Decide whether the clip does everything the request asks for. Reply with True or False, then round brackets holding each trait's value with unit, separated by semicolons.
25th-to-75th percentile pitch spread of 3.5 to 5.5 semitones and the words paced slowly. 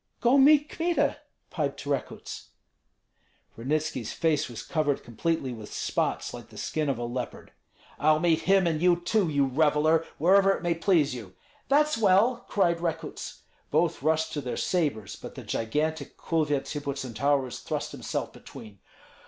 False (4.1 semitones; 150 wpm)